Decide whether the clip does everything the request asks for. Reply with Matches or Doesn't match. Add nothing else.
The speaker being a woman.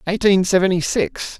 Doesn't match